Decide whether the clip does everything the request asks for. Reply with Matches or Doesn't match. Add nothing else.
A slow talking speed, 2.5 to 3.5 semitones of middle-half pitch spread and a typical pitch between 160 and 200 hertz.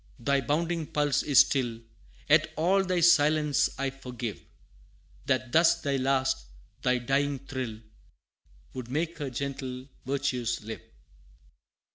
Doesn't match